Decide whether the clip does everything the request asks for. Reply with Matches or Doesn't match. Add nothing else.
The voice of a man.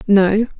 Doesn't match